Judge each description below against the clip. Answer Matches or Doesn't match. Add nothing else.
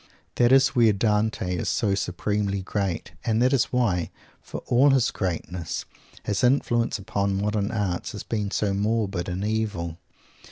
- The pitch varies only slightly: Doesn't match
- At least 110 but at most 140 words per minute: Doesn't match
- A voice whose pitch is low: Matches